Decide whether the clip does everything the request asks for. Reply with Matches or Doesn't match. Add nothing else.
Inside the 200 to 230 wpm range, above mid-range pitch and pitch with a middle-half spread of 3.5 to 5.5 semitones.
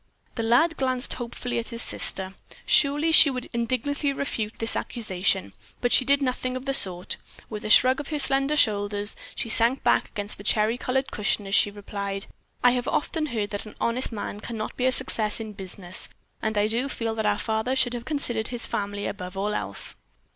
Matches